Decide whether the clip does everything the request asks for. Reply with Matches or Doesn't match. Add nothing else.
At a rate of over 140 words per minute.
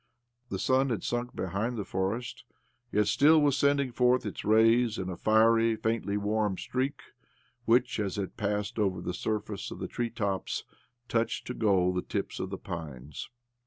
Matches